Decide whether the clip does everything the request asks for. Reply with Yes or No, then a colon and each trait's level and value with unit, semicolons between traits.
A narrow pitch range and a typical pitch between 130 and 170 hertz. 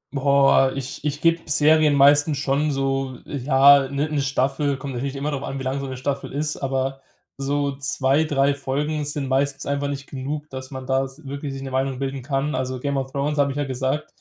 Yes: narrow, 1.3 semitones; medium, 140 Hz